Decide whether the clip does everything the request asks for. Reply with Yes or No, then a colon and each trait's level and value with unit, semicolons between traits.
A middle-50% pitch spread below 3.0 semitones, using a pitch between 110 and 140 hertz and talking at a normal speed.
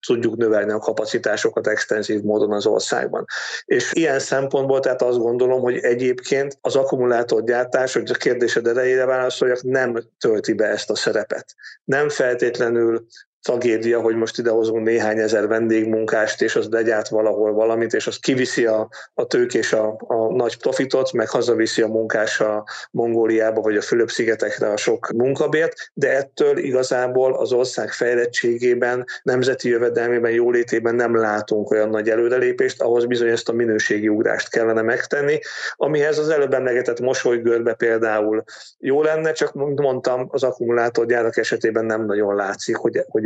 Yes: narrow, 2.5 semitones; low, 120 Hz; average, 145 wpm